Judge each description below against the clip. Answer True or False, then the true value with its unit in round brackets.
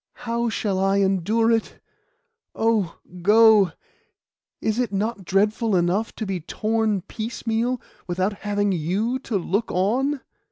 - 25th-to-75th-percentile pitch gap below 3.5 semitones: True (2.9 semitones)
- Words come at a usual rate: False (125 wpm)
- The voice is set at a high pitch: True (210 Hz)